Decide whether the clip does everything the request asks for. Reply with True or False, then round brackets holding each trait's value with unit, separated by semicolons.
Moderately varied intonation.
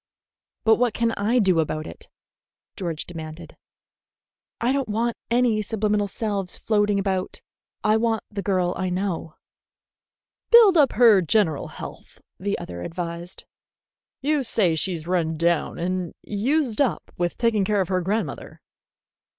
True (4.3 semitones)